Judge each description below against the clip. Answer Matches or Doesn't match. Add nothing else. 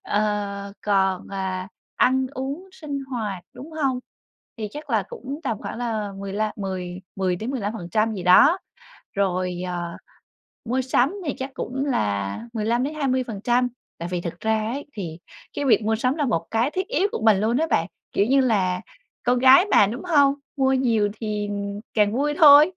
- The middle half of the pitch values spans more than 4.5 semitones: Matches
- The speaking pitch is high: Matches